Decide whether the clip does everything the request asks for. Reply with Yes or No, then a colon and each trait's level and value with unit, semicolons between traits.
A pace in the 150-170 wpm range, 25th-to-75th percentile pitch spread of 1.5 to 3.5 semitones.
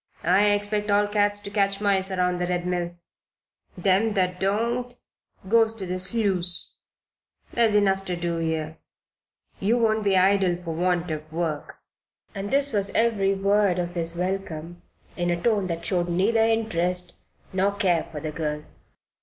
Yes: average, 160 wpm; average, 2.9 semitones